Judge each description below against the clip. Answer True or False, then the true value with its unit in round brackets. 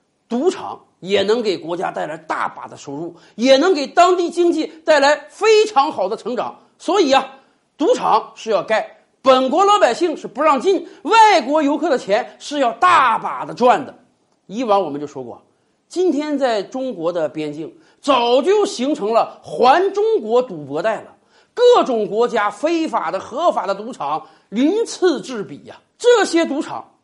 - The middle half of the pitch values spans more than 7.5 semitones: True (8.0 semitones)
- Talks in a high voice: True (290 Hz)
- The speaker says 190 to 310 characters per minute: True (240 characters per minute)